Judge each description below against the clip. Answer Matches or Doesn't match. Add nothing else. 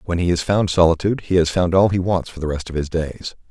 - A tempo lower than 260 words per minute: Doesn't match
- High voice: Doesn't match